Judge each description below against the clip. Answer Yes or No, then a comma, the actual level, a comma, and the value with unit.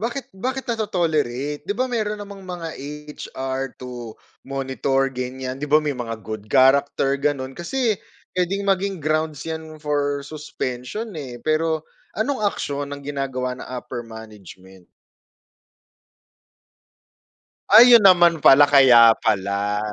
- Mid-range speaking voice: Yes, medium, 145 Hz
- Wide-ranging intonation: Yes, wide, 5.9 semitones